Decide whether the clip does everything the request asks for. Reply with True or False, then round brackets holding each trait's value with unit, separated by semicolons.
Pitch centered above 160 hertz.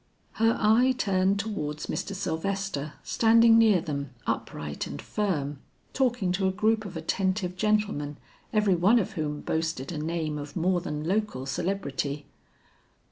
True (185 Hz)